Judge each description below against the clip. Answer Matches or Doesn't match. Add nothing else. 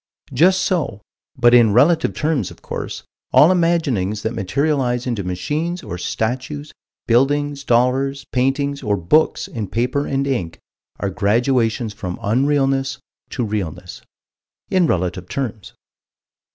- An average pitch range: Matches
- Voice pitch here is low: Matches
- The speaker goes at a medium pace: Doesn't match